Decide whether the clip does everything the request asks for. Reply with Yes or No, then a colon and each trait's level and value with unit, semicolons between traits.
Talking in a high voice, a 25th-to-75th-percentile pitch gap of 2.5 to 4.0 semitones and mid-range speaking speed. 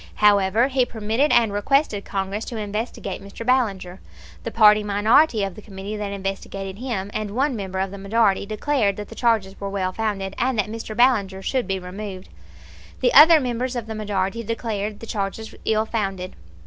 Yes: high, 210 Hz; average, 2.8 semitones; average, 180 wpm